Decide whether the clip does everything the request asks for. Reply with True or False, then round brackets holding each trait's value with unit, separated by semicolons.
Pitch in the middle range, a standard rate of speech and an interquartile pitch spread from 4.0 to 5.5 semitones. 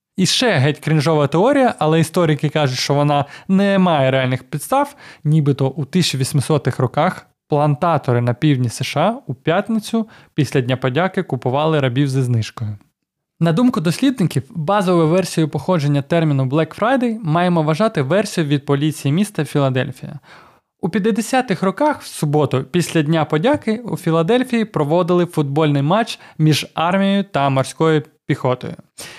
True (155 Hz; 135 wpm; 4.7 semitones)